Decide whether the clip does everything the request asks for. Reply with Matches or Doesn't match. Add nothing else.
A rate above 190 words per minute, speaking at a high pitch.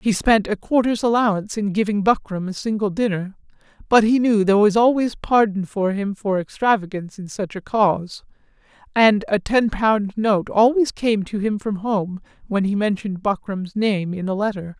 Doesn't match